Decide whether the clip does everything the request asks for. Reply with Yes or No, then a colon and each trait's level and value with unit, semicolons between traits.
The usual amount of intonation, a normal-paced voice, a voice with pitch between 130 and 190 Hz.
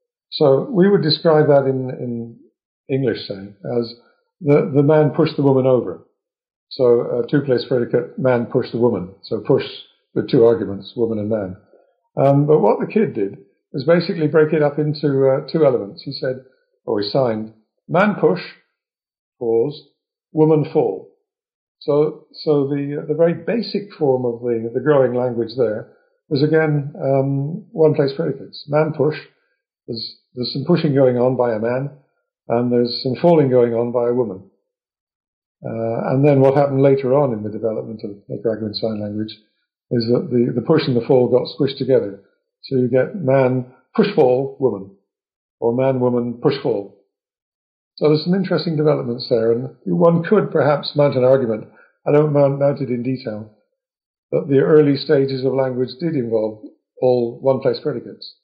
Yes: average, 4.2 semitones; average, 165 wpm; low, 135 Hz